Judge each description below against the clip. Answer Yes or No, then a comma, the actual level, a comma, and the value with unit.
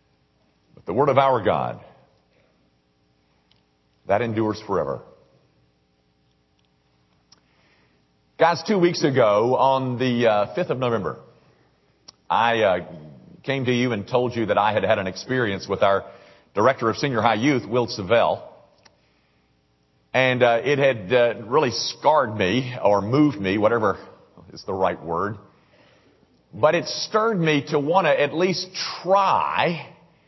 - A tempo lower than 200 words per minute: Yes, slow, 135 wpm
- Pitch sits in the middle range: No, low, 110 Hz